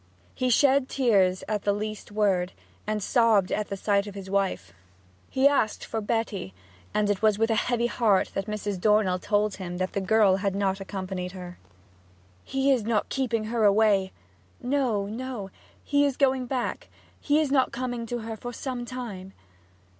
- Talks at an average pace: Yes, average, 175 wpm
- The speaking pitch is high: Yes, high, 215 Hz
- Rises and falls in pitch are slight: No, average, 3.7 semitones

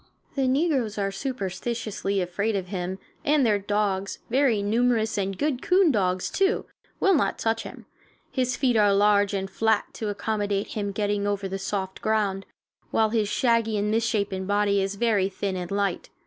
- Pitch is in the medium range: No, high, 205 Hz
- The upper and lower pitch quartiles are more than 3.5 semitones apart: No, average, 2.7 semitones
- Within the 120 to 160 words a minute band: No, average, 175 wpm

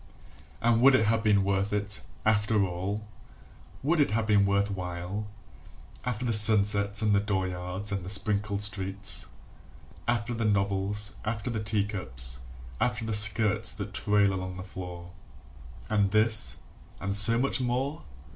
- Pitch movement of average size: No, narrow, 1.9 semitones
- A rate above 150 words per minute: No, average, 145 wpm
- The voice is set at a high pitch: No, low, 105 Hz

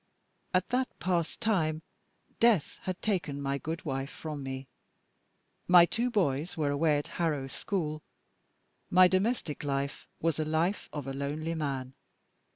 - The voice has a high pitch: No, medium, 155 Hz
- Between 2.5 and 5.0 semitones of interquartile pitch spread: Yes, average, 4.3 semitones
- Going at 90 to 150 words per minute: Yes, average, 145 wpm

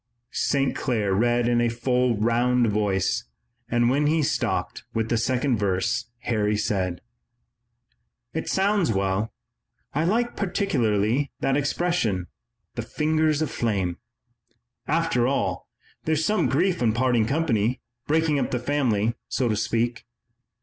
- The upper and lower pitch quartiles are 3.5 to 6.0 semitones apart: Yes, average, 5.3 semitones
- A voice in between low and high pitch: No, low, 120 Hz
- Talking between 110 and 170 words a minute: Yes, slow, 135 wpm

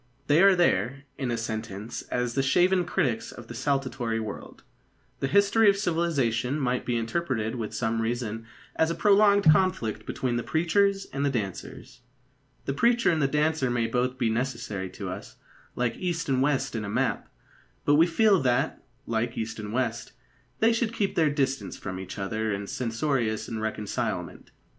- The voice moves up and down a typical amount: No, wide, 6.3 semitones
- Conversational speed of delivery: Yes, average, 170 wpm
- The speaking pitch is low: Yes, low, 130 Hz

